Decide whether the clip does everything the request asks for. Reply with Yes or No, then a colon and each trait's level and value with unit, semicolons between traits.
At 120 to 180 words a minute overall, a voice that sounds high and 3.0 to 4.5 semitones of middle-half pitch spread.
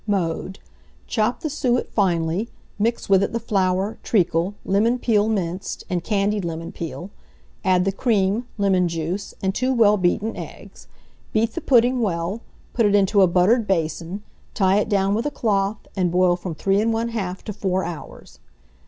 Yes: average, 165 wpm; high, 195 Hz; average, 3.4 semitones